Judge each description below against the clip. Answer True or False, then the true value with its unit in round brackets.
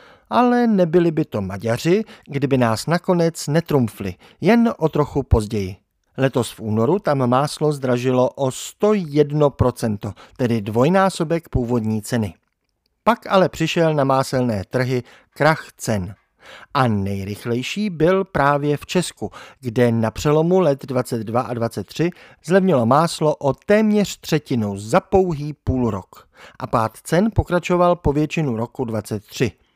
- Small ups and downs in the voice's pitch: False (6.5 semitones)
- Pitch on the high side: False (135 Hz)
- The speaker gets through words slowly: False (125 wpm)